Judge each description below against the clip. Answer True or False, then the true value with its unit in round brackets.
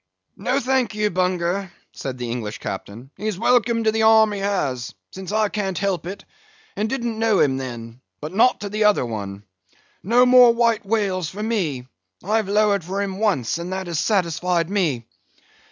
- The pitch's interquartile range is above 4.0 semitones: True (5.2 semitones)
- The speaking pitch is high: True (195 Hz)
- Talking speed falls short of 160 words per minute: False (175 wpm)